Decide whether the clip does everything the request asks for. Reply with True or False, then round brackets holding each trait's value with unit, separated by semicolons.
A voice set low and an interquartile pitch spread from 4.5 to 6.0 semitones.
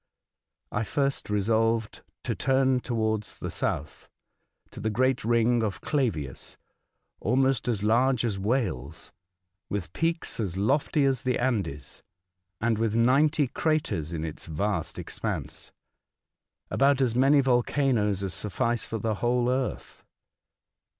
False (115 Hz; 4.1 semitones)